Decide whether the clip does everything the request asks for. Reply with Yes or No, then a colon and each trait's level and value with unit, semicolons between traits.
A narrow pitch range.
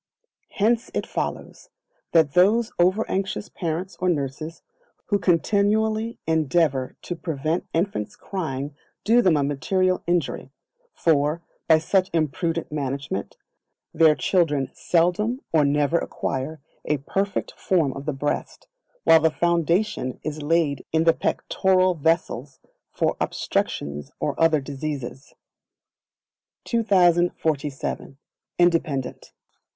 No: average, 4.2 semitones